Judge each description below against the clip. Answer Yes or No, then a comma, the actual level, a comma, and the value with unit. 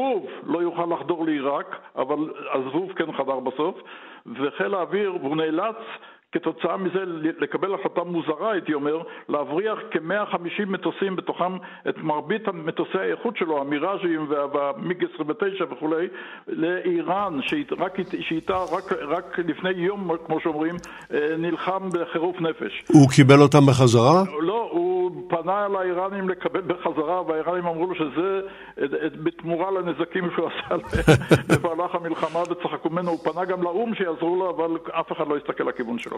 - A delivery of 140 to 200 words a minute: No, average, 130 wpm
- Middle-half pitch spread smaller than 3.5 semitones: Yes, average, 2.7 semitones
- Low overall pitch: No, medium, 170 Hz